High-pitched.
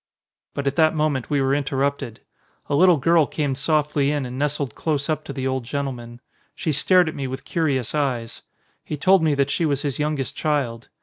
No: medium, 140 Hz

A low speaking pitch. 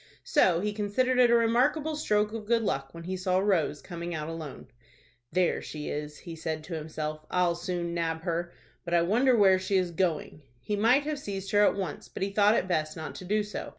No: medium, 185 Hz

